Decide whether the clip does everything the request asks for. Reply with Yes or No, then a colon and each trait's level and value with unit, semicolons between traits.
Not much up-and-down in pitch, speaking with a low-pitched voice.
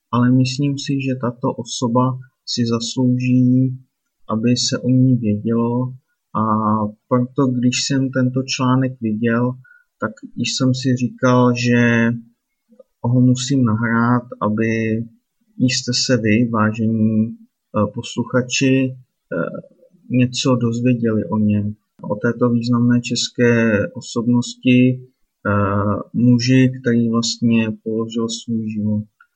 Yes: narrow, 1.9 semitones; low, 120 Hz